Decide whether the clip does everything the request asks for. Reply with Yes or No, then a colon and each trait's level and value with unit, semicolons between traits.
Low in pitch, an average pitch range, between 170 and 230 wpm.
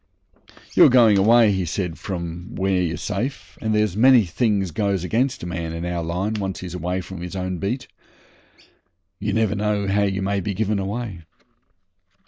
Yes: very low, 95 Hz; average, 3.1 semitones; average, 180 wpm